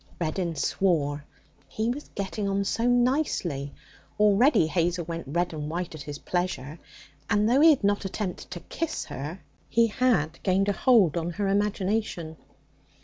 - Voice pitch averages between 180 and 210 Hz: Yes, high, 190 Hz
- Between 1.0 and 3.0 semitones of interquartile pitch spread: No, average, 4.6 semitones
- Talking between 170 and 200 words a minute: No, average, 155 wpm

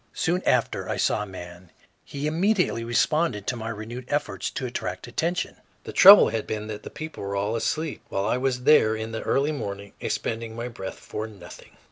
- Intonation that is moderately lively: No, wide, 5.7 semitones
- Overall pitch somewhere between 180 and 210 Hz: No, low, 115 Hz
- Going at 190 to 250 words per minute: Yes, average, 195 wpm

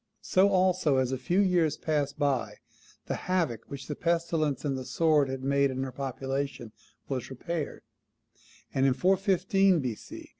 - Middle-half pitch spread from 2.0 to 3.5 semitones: No, average, 4.8 semitones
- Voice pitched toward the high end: No, medium, 145 Hz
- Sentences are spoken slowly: No, average, 155 wpm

